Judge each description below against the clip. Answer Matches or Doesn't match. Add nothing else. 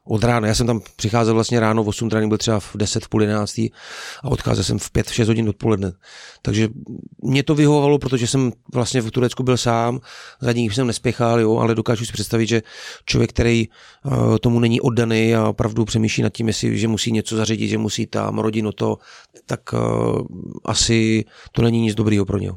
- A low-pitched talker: Matches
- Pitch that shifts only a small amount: Matches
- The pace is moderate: Doesn't match